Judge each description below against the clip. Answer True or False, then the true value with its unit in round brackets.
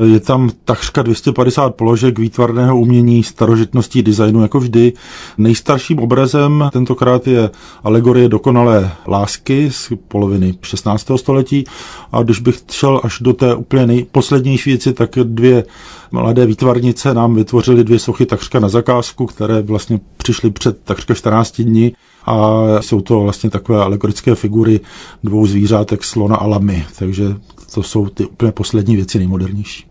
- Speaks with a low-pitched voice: True (115 Hz)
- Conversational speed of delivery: True (140 wpm)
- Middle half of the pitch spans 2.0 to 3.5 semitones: True (2.7 semitones)